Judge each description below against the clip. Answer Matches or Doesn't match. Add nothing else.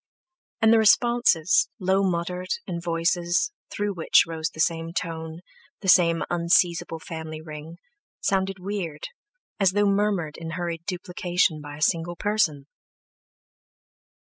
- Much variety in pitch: Doesn't match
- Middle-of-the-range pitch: Matches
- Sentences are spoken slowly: Matches